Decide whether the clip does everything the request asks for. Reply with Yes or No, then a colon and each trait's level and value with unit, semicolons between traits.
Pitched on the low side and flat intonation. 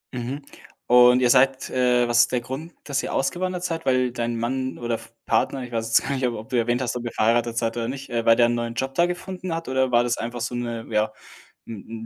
Yes: low, 120 Hz; narrow, 2.1 semitones